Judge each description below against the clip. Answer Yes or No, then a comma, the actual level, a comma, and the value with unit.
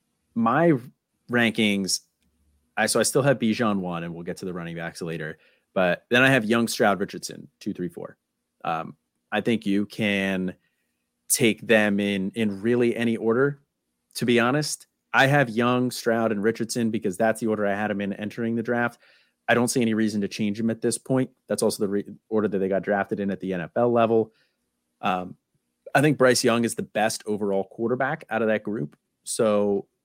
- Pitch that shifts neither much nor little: Yes, average, 3.4 semitones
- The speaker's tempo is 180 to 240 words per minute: Yes, average, 200 wpm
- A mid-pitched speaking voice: No, low, 110 Hz